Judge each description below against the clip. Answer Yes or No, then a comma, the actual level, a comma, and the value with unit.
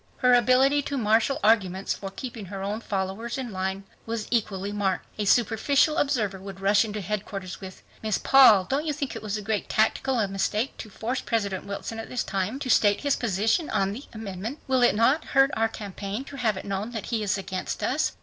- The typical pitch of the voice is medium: No, high, 215 Hz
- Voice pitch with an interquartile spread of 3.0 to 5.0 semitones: Yes, average, 4.1 semitones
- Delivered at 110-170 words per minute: No, fast, 205 wpm